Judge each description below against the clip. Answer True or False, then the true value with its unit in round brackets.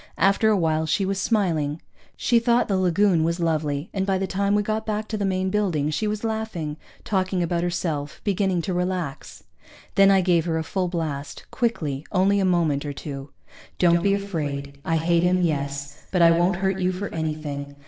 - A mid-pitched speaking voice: True (180 Hz)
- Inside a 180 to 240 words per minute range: True (200 wpm)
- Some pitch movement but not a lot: True (3.9 semitones)